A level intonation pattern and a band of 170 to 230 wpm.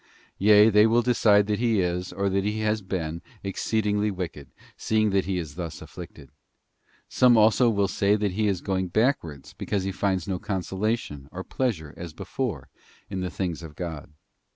No: average, 3.3 semitones; average, 185 wpm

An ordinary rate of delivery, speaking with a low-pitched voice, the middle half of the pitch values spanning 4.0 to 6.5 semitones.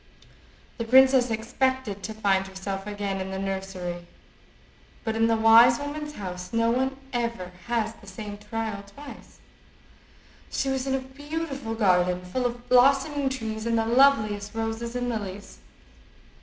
No: average, 145 wpm; high, 225 Hz; average, 4.4 semitones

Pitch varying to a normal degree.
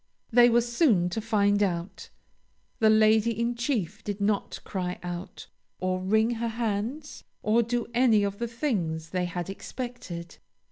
Yes: average, 4.2 semitones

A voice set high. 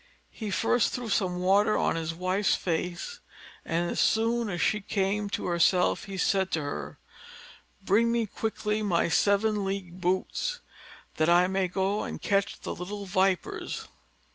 Yes: high, 195 Hz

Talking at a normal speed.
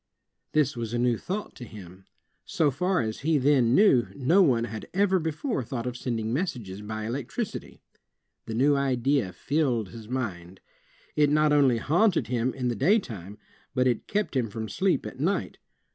Yes: average, 175 wpm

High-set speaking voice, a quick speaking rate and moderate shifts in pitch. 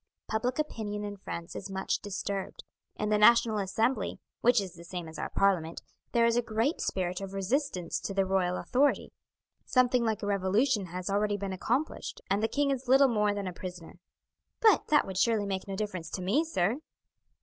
No: high, 205 Hz; average, 195 wpm; average, 4.0 semitones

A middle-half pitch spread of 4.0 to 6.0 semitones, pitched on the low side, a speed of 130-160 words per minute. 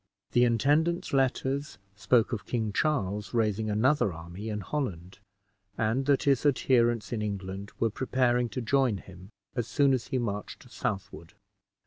Yes: average, 4.5 semitones; low, 115 Hz; average, 145 wpm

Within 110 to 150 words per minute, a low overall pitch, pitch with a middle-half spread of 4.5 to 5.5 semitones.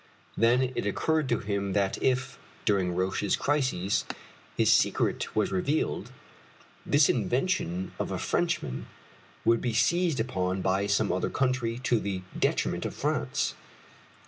Yes: slow, 135 wpm; low, 110 Hz; average, 5.2 semitones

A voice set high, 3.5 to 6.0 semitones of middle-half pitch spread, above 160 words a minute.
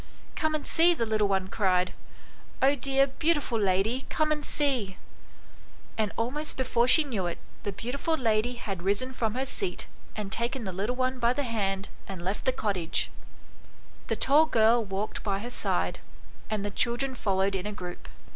Yes: high, 230 Hz; average, 5.1 semitones; average, 180 wpm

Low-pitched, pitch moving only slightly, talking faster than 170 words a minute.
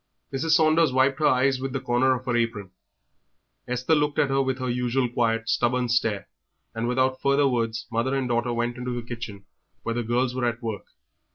Yes: low, 125 Hz; narrow, 2.0 semitones; average, 200 wpm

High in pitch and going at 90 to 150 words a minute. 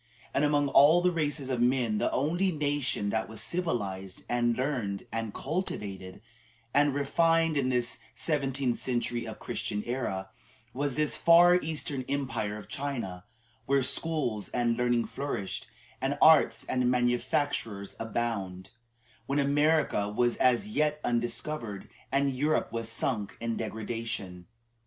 No: low, 125 Hz; slow, 135 wpm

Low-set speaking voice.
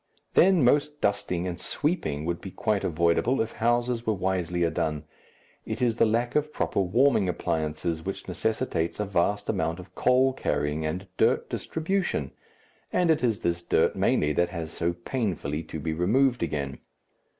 Yes: very low, 95 Hz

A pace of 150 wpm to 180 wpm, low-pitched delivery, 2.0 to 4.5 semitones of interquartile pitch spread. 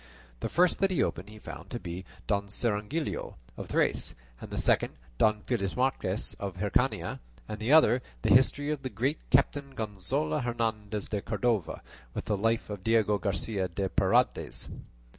Yes: average, 160 wpm; low, 110 Hz; average, 3.9 semitones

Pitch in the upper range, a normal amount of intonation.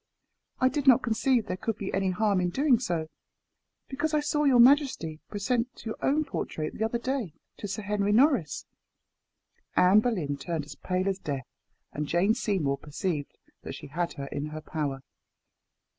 No: high, 200 Hz; wide, 7.8 semitones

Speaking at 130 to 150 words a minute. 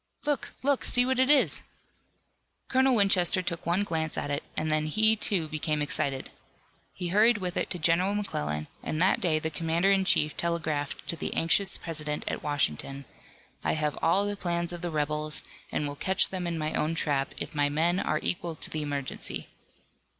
No: average, 190 wpm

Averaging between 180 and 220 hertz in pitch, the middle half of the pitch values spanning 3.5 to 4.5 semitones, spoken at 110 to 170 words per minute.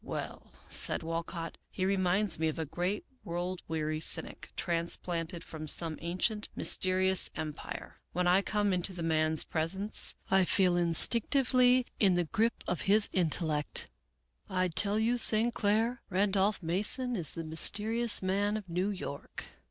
Yes: medium, 185 Hz; average, 3.9 semitones; average, 155 wpm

